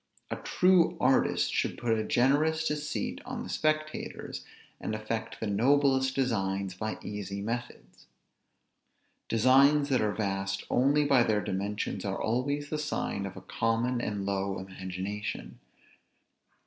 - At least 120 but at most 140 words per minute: Yes, slow, 135 wpm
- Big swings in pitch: Yes, wide, 5.8 semitones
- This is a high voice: No, low, 115 Hz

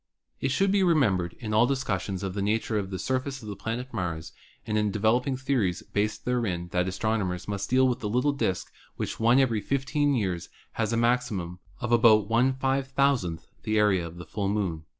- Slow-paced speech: No, average, 195 wpm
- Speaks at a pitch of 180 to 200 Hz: No, low, 110 Hz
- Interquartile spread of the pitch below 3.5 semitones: No, average, 4.9 semitones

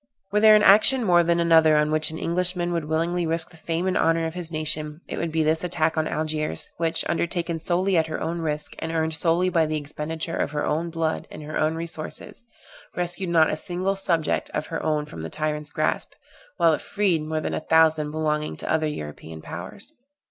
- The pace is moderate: No, fast, 215 wpm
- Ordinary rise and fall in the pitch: No, narrow, 1.8 semitones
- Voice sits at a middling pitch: Yes, medium, 160 Hz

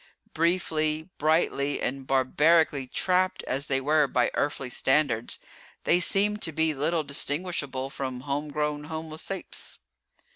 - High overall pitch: No, medium, 150 Hz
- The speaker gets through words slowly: Yes, slow, 120 wpm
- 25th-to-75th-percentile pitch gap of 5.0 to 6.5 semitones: No, average, 2.8 semitones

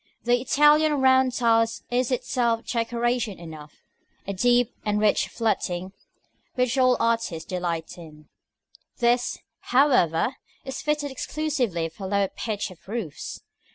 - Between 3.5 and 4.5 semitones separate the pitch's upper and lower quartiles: No, average, 5.2 semitones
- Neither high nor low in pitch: No, high, 235 Hz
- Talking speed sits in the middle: No, slow, 120 wpm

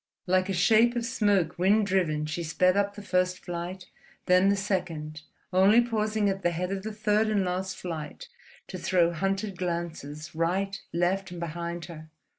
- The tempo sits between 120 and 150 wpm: No, average, 175 wpm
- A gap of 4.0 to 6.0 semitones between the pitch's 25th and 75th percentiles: No, average, 2.8 semitones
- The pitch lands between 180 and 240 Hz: Yes, medium, 185 Hz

